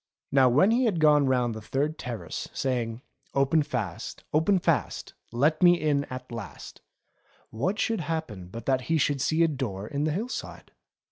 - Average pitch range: Yes, average, 4.6 semitones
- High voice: No, medium, 140 Hz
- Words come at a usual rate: Yes, average, 180 wpm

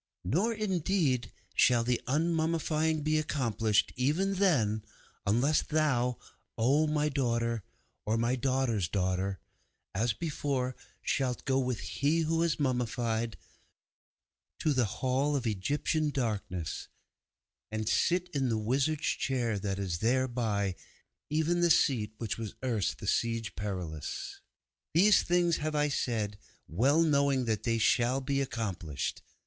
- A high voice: No, low, 130 Hz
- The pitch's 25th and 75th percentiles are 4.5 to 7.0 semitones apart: Yes, wide, 5.4 semitones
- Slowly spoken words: Yes, slow, 130 wpm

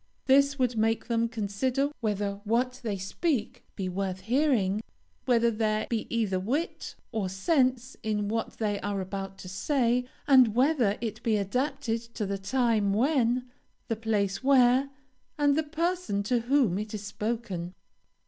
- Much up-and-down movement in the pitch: No, average, 4.2 semitones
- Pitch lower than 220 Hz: No, high, 230 Hz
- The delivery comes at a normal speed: Yes, average, 150 wpm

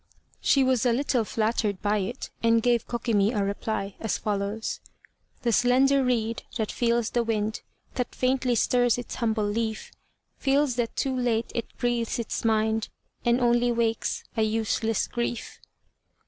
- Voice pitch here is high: Yes, high, 230 Hz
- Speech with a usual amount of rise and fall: No, narrow, 1.9 semitones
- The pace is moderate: Yes, average, 150 wpm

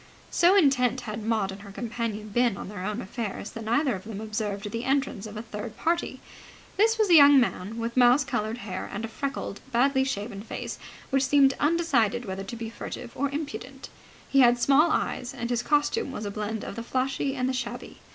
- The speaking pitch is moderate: No, high, 240 Hz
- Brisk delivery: Yes, fast, 210 wpm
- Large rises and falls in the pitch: No, average, 4.2 semitones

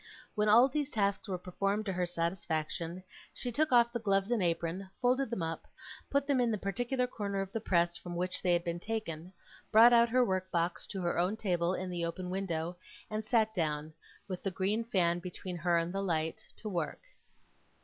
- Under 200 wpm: No, fast, 205 wpm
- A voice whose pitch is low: No, high, 190 Hz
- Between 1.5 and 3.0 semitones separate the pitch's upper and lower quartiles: No, average, 4.3 semitones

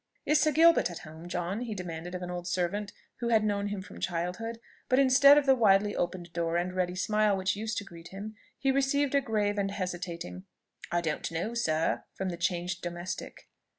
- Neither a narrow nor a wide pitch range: Yes, average, 4.3 semitones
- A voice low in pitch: No, high, 190 Hz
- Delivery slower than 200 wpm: No, fast, 205 wpm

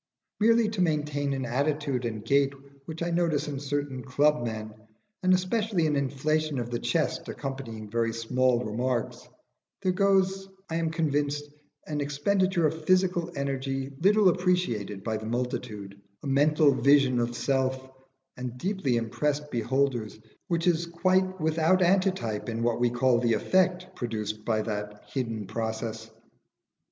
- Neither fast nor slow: Yes, average, 145 wpm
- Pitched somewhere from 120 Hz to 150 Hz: Yes, medium, 140 Hz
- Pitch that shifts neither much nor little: No, wide, 6.0 semitones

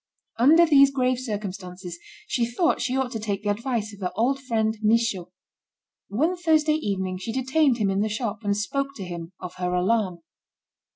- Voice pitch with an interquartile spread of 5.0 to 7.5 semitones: Yes, average, 5.3 semitones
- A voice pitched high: Yes, high, 220 Hz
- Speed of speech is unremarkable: Yes, average, 180 wpm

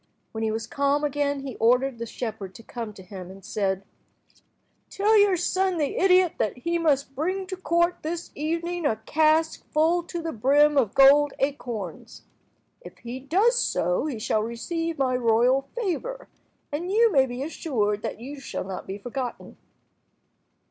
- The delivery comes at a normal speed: Yes, average, 170 wpm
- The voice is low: No, very high, 280 Hz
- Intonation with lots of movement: Yes, wide, 6.6 semitones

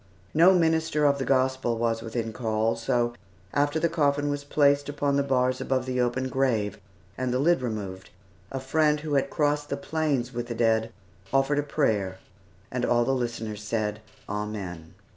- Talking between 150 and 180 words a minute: Yes, average, 175 wpm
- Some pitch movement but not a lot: Yes, average, 4.2 semitones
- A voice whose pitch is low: Yes, low, 130 Hz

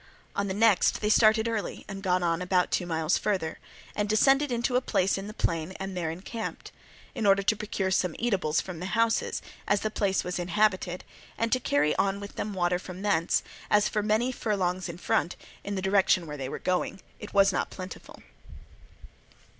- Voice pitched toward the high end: Yes, high, 195 Hz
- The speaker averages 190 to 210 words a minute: Yes, average, 200 wpm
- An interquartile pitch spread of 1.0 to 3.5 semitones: Yes, average, 3.0 semitones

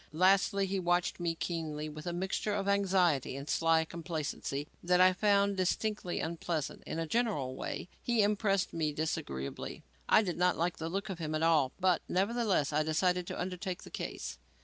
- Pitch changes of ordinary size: Yes, average, 3.6 semitones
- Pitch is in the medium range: Yes, medium, 175 Hz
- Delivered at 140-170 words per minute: No, average, 180 wpm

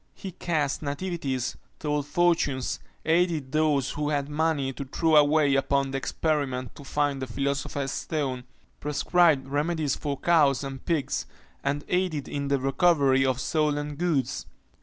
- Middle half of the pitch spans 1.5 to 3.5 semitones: Yes, narrow, 2.5 semitones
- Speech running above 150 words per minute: No, average, 140 wpm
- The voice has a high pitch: No, medium, 145 Hz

